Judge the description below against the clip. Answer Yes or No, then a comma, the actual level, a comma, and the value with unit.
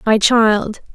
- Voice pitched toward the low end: No, high, 220 Hz